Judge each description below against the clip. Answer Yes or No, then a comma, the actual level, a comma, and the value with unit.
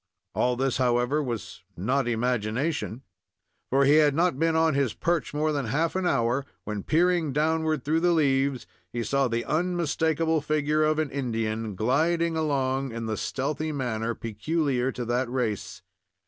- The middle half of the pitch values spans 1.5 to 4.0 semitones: No, average, 4.5 semitones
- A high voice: No, medium, 140 Hz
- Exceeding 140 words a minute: Yes, average, 160 wpm